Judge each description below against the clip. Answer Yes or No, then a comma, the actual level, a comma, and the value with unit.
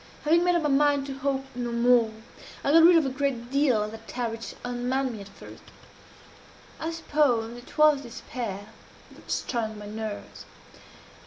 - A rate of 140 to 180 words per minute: Yes, average, 175 wpm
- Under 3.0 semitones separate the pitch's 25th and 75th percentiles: No, average, 4.0 semitones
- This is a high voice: Yes, very high, 250 Hz